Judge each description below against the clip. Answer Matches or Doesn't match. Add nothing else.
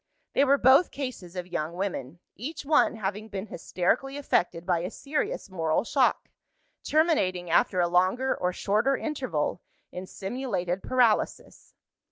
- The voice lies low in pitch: Doesn't match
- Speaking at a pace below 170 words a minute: Matches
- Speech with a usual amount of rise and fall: Doesn't match